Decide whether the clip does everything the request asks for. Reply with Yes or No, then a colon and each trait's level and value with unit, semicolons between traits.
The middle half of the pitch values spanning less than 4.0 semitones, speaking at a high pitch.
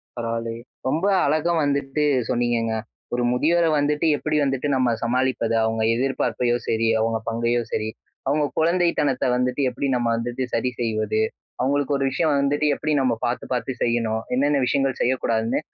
No: average, 3.6 semitones; low, 125 Hz